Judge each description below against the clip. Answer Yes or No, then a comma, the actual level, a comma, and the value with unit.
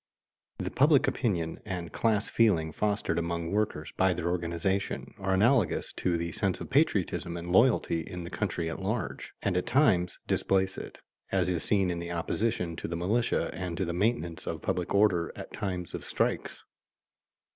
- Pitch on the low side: Yes, very low, 90 Hz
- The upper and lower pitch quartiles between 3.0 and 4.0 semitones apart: Yes, average, 3.4 semitones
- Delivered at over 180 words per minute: No, average, 175 wpm